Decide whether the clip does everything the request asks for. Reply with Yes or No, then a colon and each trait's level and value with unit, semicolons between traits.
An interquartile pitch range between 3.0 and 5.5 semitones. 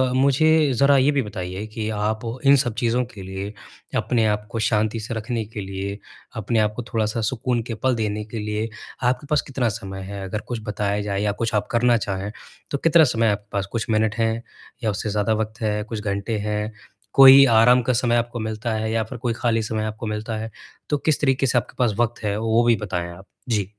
No: narrow, 2.4 semitones